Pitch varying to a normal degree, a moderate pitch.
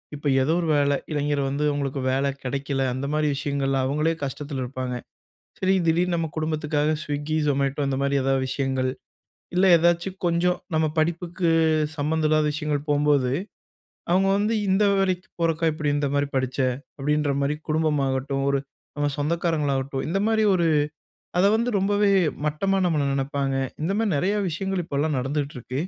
Yes: average, 3.4 semitones; medium, 150 Hz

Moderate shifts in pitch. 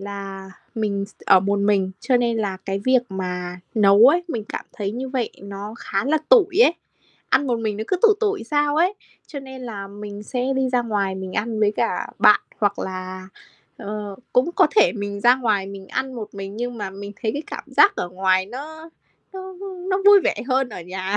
Yes: average, 5.0 semitones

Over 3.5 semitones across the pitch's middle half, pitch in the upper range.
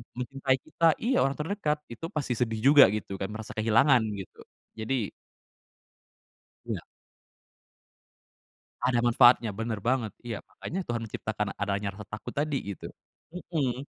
No: average, 4.6 semitones; low, 120 Hz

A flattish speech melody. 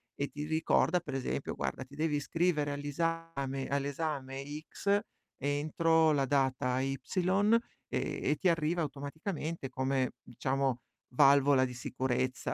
No: average, 3.1 semitones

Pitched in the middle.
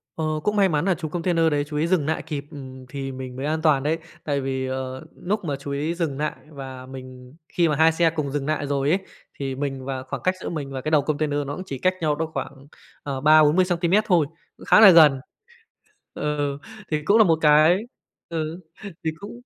Yes: medium, 150 Hz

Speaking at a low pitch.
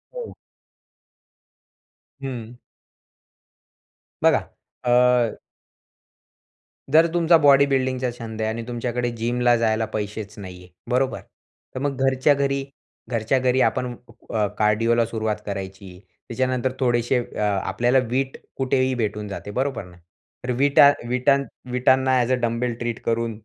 Yes: low, 120 Hz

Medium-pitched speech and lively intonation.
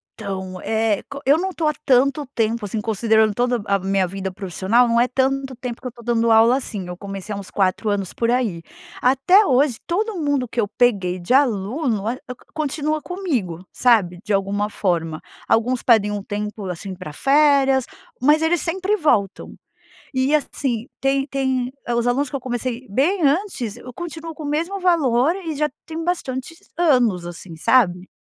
No: high, 245 Hz; wide, 5.8 semitones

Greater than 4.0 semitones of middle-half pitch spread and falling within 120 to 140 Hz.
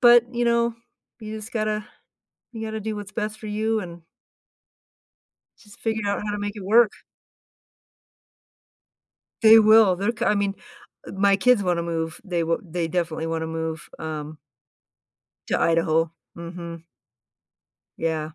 No: average, 4.6 semitones; high, 200 Hz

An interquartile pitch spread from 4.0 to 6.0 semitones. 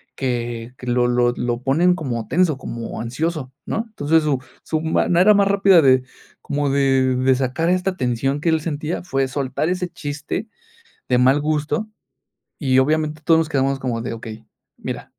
Yes: average, 4.3 semitones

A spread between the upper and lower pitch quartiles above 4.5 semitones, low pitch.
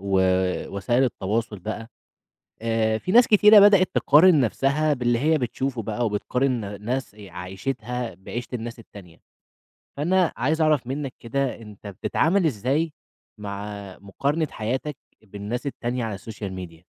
Yes: wide, 5.4 semitones; low, 120 Hz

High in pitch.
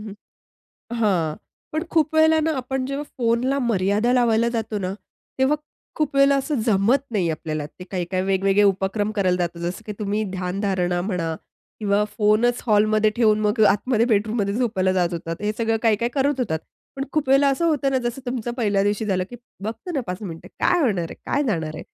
Yes: high, 215 Hz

